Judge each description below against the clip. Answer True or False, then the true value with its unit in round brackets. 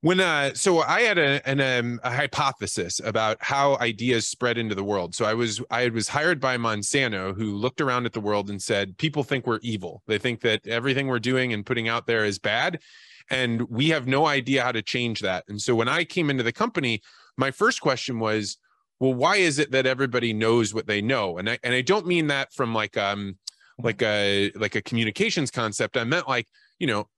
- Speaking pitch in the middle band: False (120 Hz)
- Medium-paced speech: False (225 wpm)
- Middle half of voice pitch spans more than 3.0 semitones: True (3.8 semitones)